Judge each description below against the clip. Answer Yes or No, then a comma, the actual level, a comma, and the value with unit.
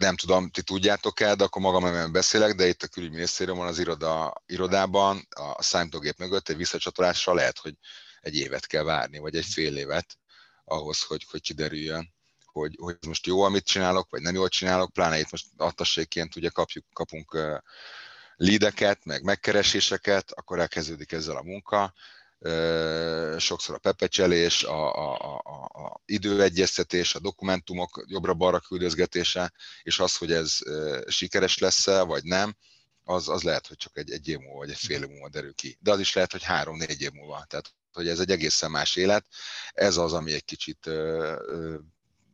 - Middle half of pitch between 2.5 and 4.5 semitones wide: Yes, average, 2.8 semitones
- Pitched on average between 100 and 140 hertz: No, very low, 90 Hz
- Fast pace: Yes, fast, 170 wpm